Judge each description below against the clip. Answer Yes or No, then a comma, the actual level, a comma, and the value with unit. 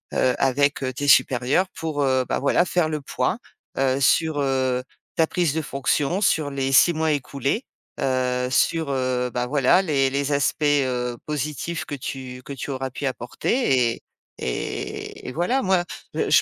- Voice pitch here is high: No, medium, 140 Hz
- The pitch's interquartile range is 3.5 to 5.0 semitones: No, average, 3.1 semitones